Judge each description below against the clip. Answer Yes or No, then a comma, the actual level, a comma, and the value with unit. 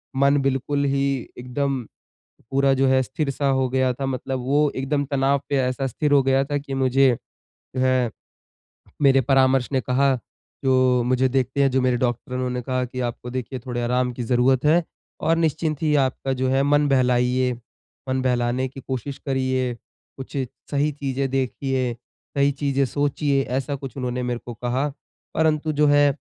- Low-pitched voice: Yes, low, 130 Hz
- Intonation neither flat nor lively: No, narrow, 1.6 semitones